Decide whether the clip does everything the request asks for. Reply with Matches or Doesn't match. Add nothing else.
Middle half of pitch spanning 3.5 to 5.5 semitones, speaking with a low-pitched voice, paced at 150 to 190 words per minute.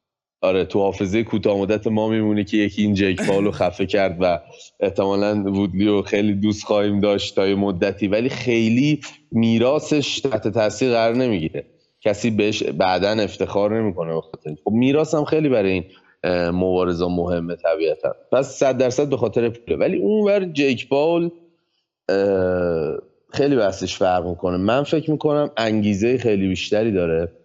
Matches